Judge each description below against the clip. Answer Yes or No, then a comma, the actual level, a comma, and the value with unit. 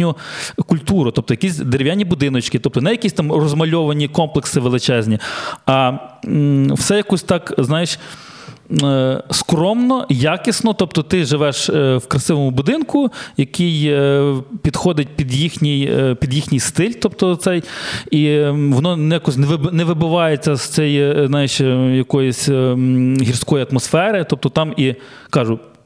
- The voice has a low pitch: No, medium, 150 Hz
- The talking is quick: No, average, 115 wpm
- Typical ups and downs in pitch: Yes, average, 3.9 semitones